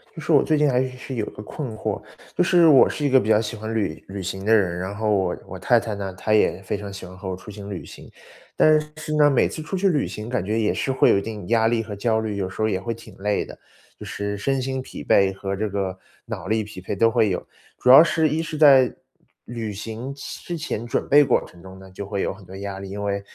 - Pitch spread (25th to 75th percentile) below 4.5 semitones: No, average, 5.1 semitones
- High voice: No, low, 110 Hz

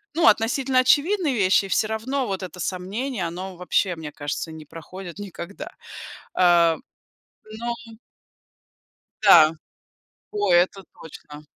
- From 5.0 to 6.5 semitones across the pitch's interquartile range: Yes, wide, 5.4 semitones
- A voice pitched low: No, high, 195 Hz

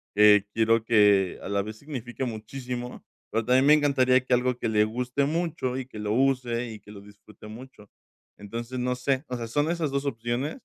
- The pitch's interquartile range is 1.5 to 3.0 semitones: No, average, 3.4 semitones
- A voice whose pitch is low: Yes, low, 125 Hz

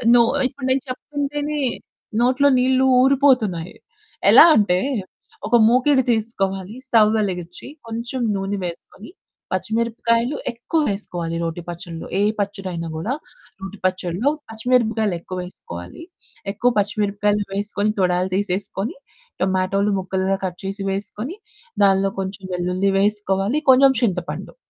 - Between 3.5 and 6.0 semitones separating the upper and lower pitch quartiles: Yes, average, 4.2 semitones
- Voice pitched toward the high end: Yes, high, 205 Hz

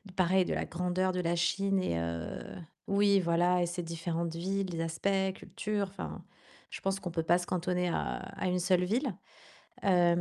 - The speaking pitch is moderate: Yes, medium, 180 Hz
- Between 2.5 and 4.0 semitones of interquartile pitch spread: No, narrow, 2.0 semitones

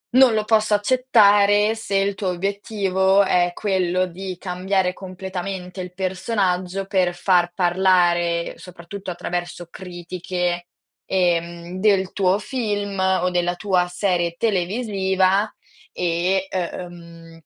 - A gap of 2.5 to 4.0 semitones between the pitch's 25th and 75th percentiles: No, narrow, 2.1 semitones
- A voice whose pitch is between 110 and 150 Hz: No, medium, 185 Hz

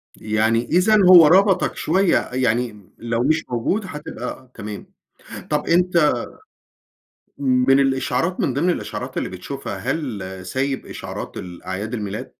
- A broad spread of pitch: Yes, wide, 6.6 semitones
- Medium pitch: No, low, 130 Hz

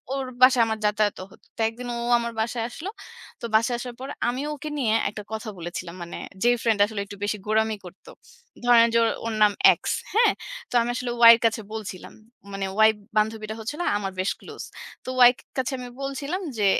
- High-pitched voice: Yes, high, 225 Hz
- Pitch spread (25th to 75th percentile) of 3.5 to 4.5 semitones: No, average, 2.8 semitones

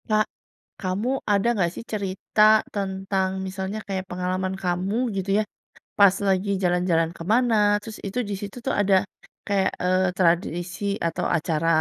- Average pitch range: No, narrow, 1.9 semitones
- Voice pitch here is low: No, high, 190 Hz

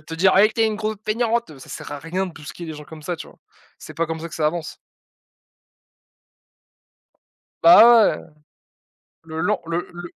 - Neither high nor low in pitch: Yes, medium, 170 Hz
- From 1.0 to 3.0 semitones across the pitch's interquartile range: No, average, 5.0 semitones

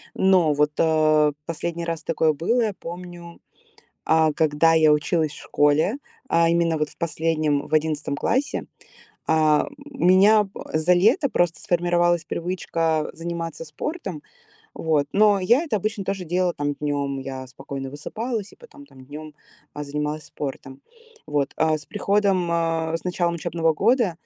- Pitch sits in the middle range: Yes, medium, 165 Hz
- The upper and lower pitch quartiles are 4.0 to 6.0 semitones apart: No, average, 3.2 semitones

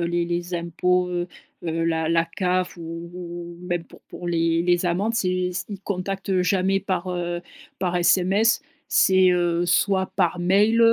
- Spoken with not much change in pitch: Yes, narrow, 1.4 semitones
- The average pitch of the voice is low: No, medium, 180 Hz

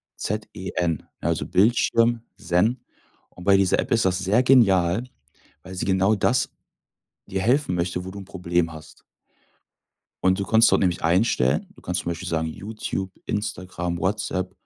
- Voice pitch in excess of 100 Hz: No, very low, 95 Hz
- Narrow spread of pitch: No, average, 3.4 semitones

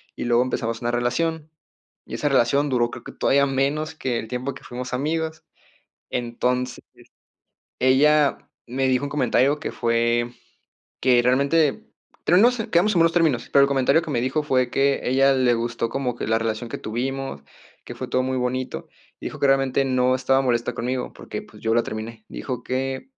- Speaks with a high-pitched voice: No, low, 130 Hz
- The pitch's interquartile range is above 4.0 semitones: No, narrow, 2.6 semitones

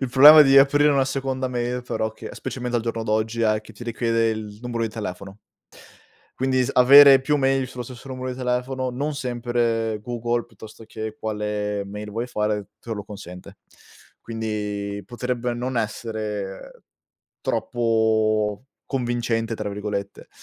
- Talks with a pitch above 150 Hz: No, low, 115 Hz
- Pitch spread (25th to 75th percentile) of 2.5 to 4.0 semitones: Yes, average, 2.9 semitones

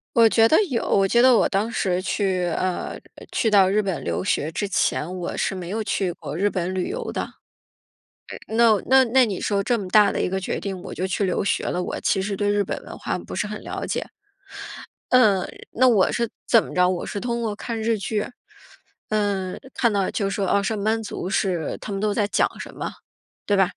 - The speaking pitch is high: Yes, high, 200 Hz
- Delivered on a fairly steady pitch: No, average, 3.0 semitones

